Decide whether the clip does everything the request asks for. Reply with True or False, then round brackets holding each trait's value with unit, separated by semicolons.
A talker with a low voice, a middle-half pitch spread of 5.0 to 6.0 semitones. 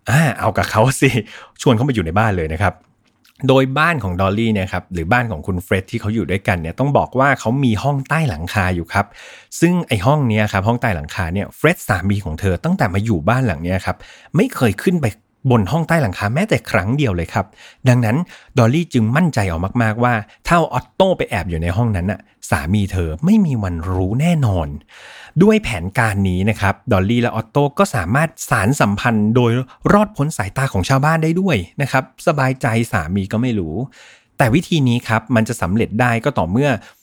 True (115 Hz; 5.5 semitones)